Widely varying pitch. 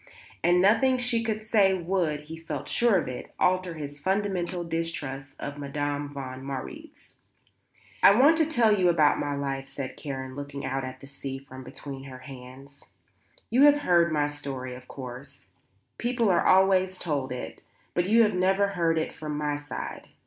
Yes: wide, 5.7 semitones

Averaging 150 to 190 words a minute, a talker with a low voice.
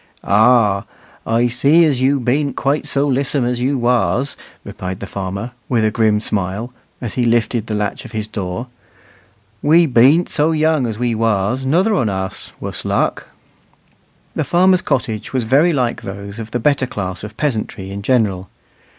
Yes: average, 170 wpm; low, 120 Hz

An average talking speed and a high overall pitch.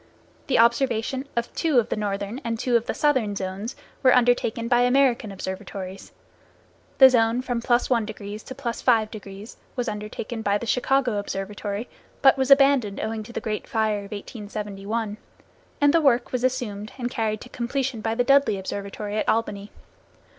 Yes: average, 160 wpm; high, 230 Hz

